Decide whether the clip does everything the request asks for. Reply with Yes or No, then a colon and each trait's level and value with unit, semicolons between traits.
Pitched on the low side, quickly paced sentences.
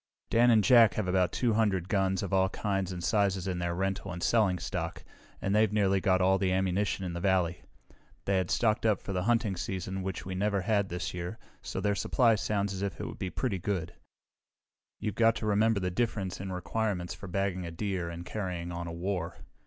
Yes: very low, 95 Hz; fast, 215 wpm